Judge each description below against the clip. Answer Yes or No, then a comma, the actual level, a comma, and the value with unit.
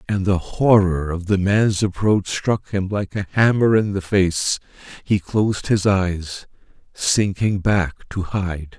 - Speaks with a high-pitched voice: No, very low, 95 Hz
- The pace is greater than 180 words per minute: No, average, 155 wpm